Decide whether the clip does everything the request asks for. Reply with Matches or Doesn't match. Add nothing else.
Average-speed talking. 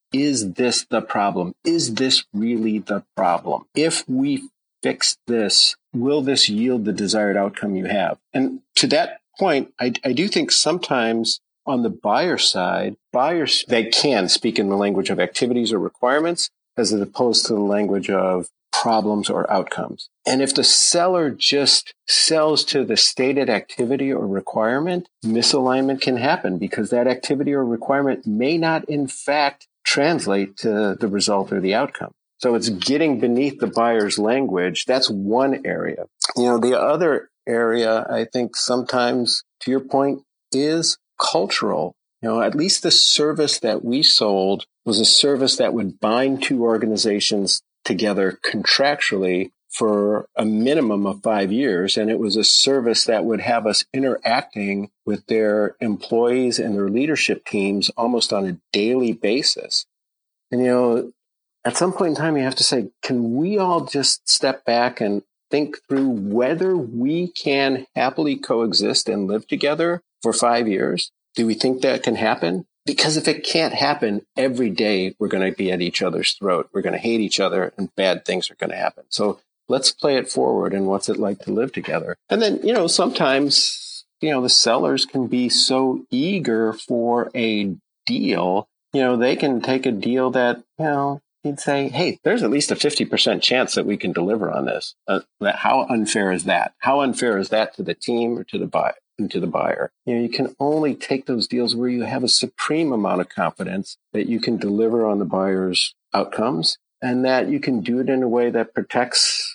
Matches